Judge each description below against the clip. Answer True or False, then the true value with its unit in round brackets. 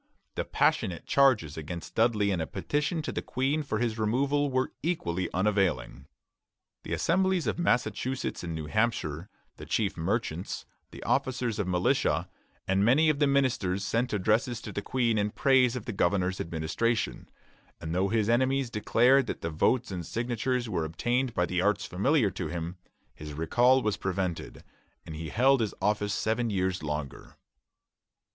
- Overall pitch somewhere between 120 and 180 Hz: False (110 Hz)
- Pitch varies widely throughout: True (6.0 semitones)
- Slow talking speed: False (165 wpm)